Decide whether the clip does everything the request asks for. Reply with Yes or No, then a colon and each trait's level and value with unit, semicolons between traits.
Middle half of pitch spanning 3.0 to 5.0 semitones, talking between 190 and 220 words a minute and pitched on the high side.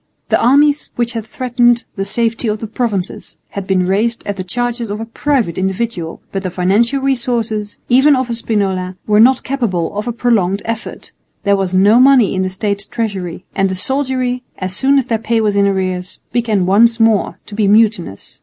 Yes: average, 3.8 semitones; average, 195 wpm; high, 220 Hz